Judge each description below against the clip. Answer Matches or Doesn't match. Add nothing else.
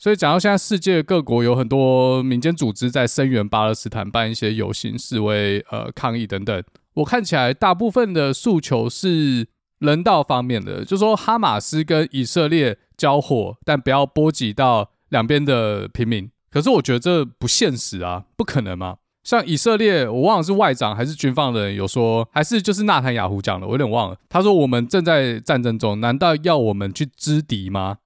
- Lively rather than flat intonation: Matches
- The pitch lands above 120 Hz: Matches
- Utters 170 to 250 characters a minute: Doesn't match